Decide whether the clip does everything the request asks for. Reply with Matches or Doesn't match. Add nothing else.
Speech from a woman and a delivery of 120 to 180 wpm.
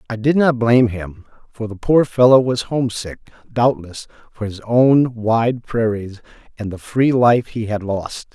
Doesn't match